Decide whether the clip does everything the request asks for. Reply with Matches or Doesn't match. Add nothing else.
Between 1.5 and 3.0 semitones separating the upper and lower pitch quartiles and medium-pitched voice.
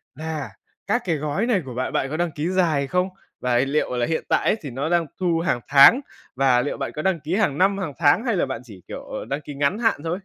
Doesn't match